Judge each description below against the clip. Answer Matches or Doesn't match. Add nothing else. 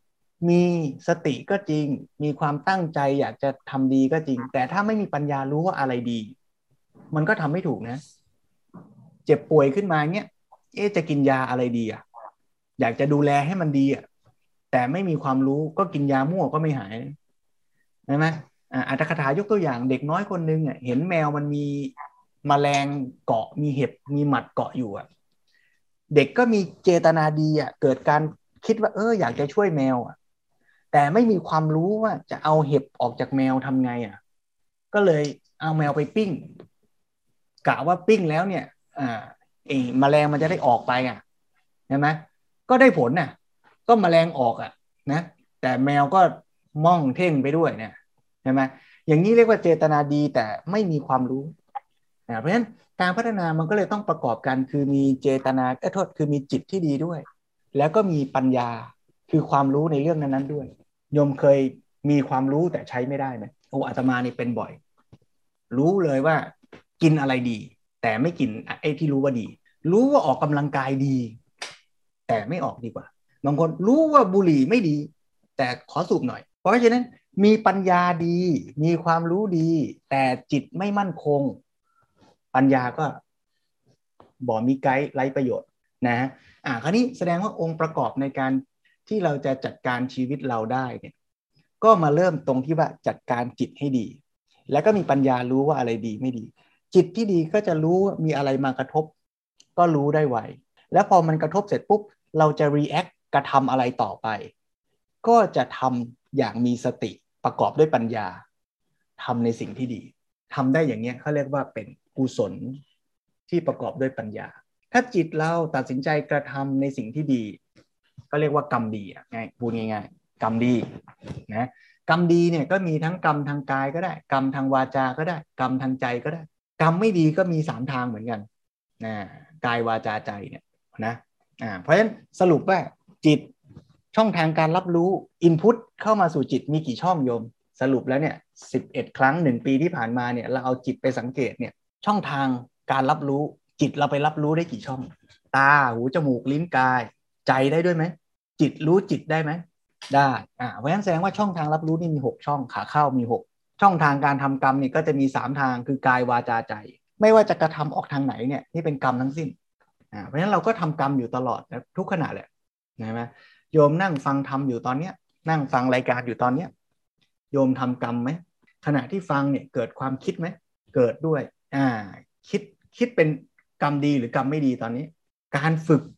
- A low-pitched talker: Doesn't match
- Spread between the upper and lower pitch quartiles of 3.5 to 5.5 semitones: Matches